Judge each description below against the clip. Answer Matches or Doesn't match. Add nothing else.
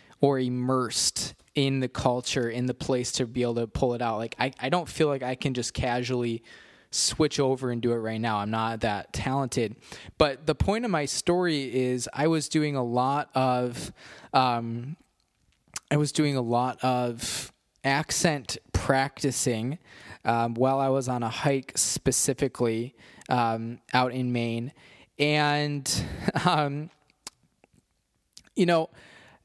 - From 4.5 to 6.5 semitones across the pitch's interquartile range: Doesn't match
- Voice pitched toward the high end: Doesn't match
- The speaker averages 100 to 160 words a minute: Matches